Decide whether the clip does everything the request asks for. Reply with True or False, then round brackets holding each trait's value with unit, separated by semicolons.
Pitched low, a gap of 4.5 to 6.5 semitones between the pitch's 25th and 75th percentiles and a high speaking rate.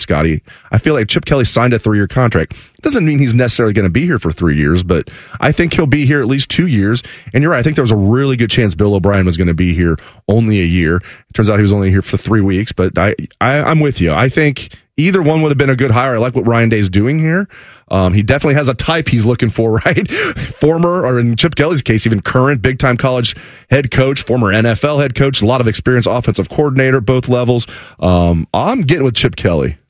True (120 Hz; 5.1 semitones; 255 wpm)